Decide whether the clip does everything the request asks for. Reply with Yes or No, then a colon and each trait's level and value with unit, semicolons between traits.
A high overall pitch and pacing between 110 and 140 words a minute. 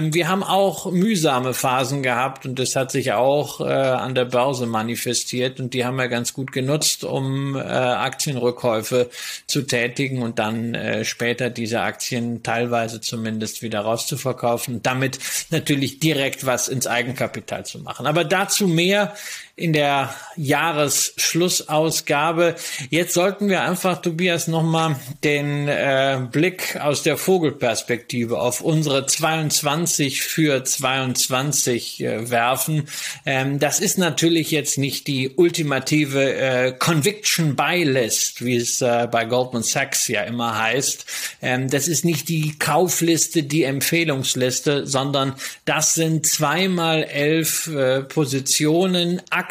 No: medium, 140 Hz; average, 130 wpm